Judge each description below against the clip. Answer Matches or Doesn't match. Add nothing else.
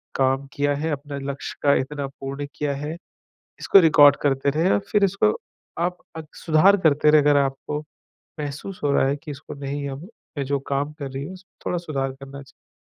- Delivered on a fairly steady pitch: Matches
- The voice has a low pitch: Doesn't match